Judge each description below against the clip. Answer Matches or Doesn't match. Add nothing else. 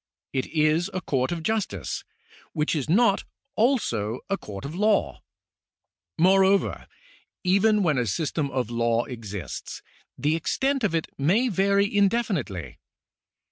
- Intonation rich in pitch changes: Matches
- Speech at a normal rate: Doesn't match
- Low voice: Doesn't match